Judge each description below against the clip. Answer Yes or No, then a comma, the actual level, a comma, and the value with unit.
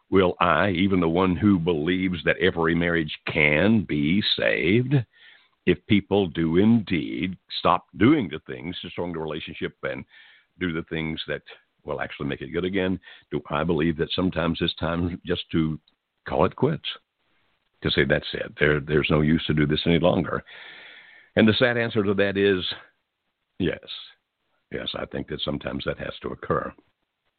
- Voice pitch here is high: No, very low, 85 Hz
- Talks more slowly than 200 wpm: Yes, average, 170 wpm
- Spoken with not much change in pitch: No, average, 3.3 semitones